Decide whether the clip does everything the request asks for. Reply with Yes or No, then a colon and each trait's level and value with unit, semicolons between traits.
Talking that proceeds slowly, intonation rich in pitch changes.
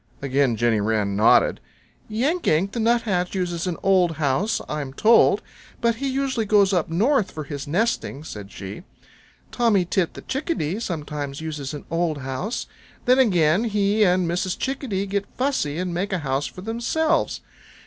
No: average, 160 wpm; wide, 7.0 semitones